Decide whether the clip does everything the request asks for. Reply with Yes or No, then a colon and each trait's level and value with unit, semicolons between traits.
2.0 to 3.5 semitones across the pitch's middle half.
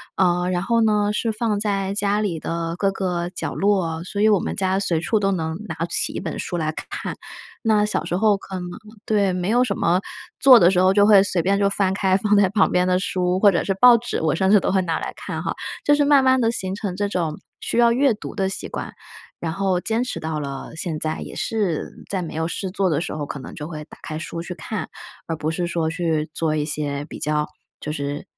No: average, 3.9 semitones